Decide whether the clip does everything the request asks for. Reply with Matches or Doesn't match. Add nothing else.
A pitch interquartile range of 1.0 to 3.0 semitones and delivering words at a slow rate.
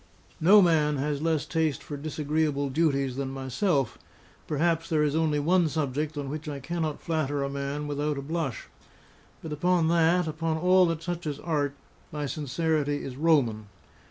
Doesn't match